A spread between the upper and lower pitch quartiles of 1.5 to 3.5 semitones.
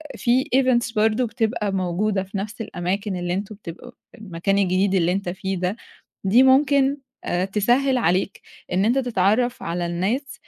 No: average, 4.6 semitones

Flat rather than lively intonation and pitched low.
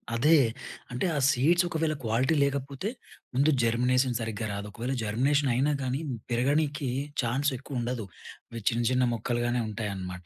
No: average, 3.4 semitones; low, 125 Hz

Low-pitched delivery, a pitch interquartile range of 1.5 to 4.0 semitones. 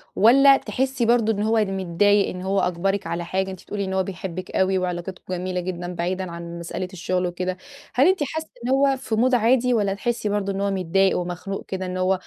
No: high, 190 Hz; average, 3.5 semitones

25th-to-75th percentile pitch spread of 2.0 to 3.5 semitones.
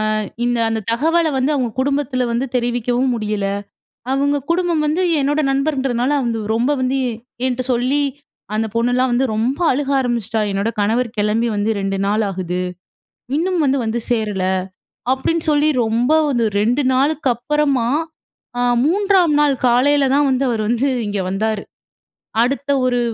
No: average, 3.9 semitones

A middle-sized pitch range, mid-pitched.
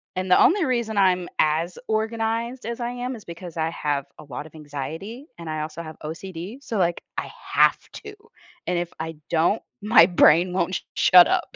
No: wide, 5.7 semitones; medium, 180 Hz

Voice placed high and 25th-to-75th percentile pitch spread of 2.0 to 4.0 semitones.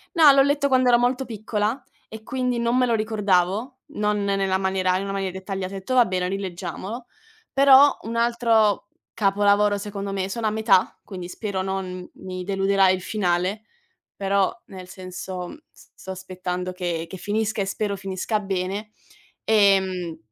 Yes: high, 200 Hz; average, 2.9 semitones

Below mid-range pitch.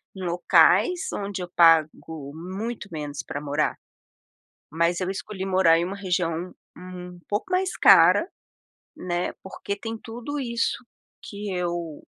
No: medium, 185 Hz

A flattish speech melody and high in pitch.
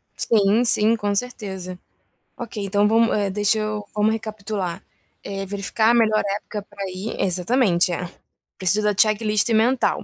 Yes: narrow, 2.0 semitones; high, 210 Hz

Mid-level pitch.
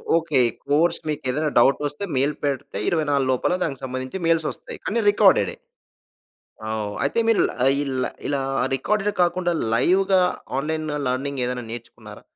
Yes: medium, 145 Hz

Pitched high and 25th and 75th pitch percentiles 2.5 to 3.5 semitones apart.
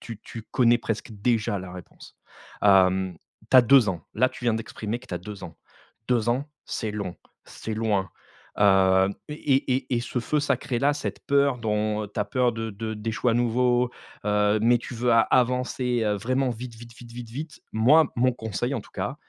No: low, 115 Hz; average, 3.2 semitones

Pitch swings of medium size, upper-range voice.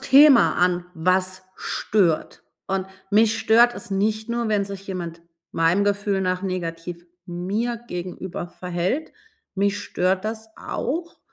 Yes: average, 3.4 semitones; high, 195 Hz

